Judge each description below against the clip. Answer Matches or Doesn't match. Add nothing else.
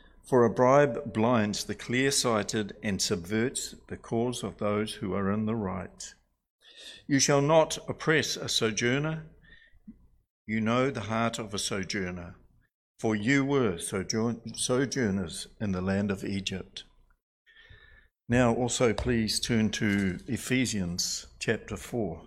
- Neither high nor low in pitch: Doesn't match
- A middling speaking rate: Doesn't match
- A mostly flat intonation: Doesn't match